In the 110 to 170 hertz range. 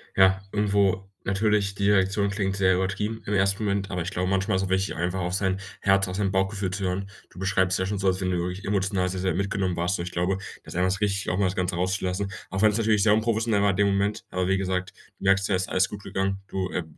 No: very low, 95 Hz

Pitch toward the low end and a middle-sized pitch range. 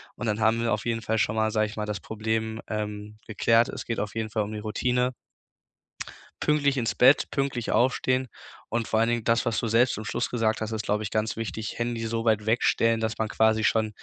No: low, 110 Hz; narrow, 1.6 semitones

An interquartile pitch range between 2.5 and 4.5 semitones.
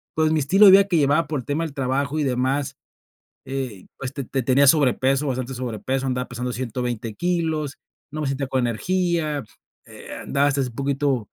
Yes: average, 3.0 semitones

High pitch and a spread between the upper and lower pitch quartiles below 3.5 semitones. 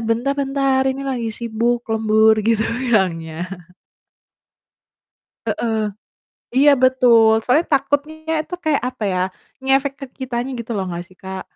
No: high, 240 Hz; average, 3.8 semitones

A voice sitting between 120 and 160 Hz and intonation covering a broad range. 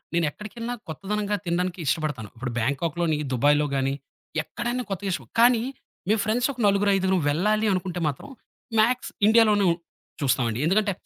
No: high, 190 Hz; wide, 6.3 semitones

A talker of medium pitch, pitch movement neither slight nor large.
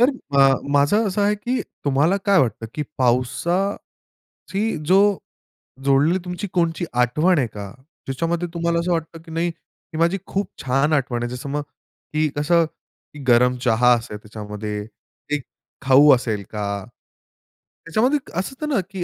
No: medium, 150 Hz; wide, 6.1 semitones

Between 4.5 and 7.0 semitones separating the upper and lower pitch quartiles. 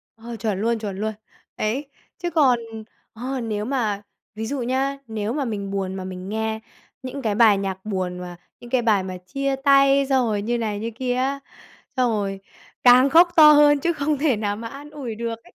Yes: average, 4.8 semitones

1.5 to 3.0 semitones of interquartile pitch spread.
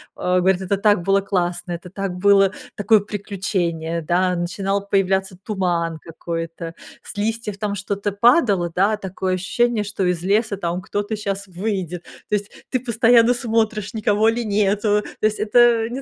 Yes: average, 2.7 semitones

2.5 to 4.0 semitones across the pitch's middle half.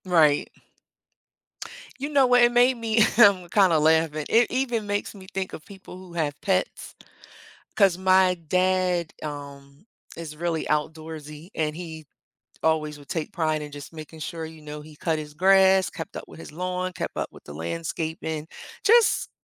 Yes: average, 3.7 semitones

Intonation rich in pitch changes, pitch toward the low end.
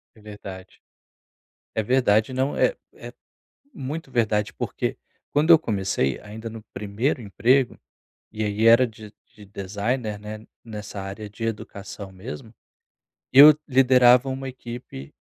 No: average, 3.8 semitones; low, 110 Hz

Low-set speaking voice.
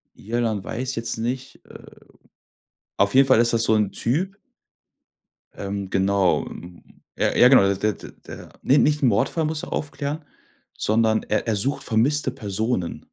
Yes: low, 115 Hz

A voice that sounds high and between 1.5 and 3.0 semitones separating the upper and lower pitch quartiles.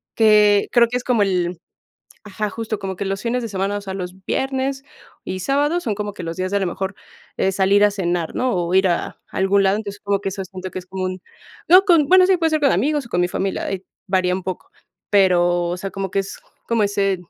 No: high, 195 Hz; average, 3.6 semitones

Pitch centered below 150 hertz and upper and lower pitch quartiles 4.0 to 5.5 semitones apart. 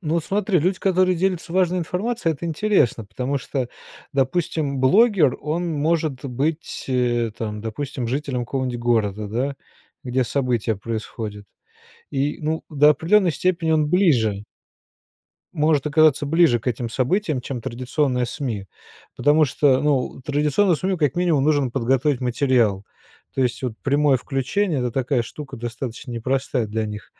Yes: medium, 140 Hz; average, 4.7 semitones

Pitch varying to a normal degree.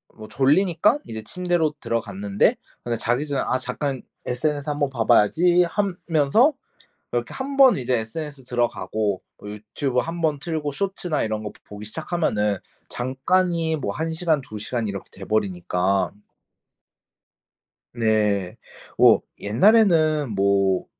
No: wide, 7.3 semitones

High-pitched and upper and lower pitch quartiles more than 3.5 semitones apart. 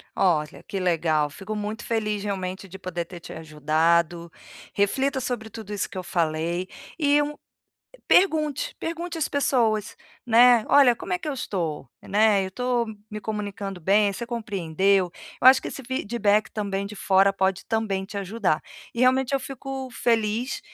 Yes: high, 210 Hz; average, 4.8 semitones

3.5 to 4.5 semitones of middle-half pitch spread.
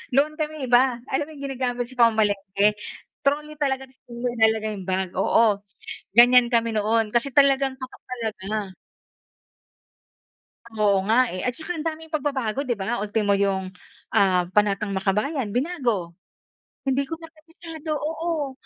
No: average, 5.0 semitones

